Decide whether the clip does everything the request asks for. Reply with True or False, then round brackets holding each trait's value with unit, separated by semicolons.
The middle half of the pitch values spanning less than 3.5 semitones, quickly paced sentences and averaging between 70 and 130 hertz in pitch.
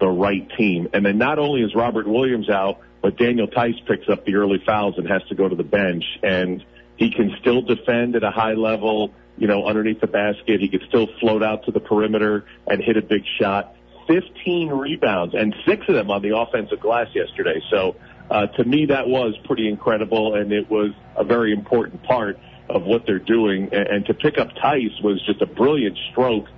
True (2.9 semitones; 210 wpm; 110 Hz)